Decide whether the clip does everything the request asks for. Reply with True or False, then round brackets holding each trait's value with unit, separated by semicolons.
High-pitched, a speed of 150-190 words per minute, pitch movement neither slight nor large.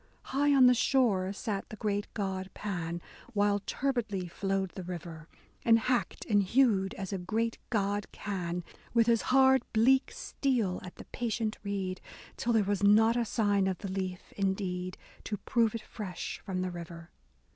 True (205 Hz; 170 wpm; 3.6 semitones)